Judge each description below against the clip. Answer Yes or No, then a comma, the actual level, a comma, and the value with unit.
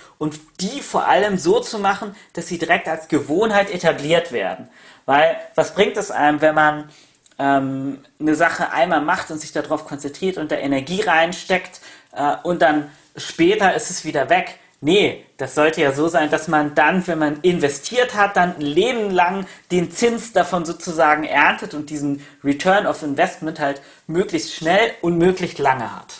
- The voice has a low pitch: No, medium, 160 Hz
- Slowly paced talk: No, average, 175 wpm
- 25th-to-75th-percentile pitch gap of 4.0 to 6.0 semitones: No, average, 3.6 semitones